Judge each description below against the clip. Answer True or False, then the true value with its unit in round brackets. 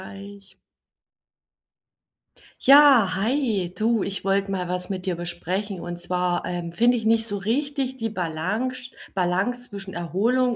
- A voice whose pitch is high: True (200 Hz)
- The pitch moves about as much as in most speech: True (4.8 semitones)